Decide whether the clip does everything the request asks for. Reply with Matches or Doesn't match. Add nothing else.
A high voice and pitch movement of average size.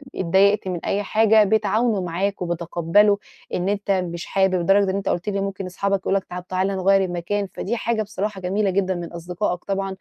Doesn't match